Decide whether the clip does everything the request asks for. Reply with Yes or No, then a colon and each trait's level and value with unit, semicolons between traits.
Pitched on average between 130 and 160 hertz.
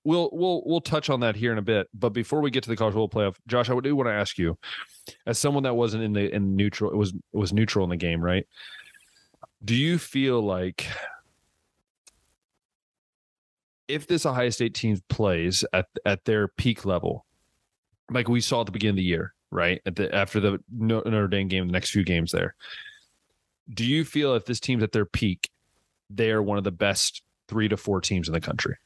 No: low, 105 Hz